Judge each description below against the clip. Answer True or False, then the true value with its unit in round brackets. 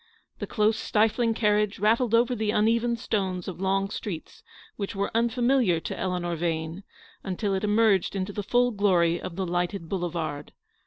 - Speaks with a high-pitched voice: True (200 Hz)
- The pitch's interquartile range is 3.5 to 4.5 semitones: True (3.9 semitones)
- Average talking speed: True (165 wpm)